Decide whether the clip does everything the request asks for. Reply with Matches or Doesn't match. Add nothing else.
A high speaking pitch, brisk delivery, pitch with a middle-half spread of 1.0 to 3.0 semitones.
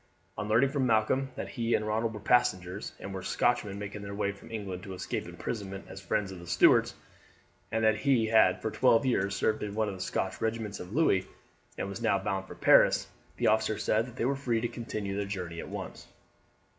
Doesn't match